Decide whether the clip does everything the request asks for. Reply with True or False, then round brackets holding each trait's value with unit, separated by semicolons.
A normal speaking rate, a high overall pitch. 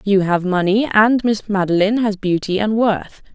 True (180 wpm; 205 Hz)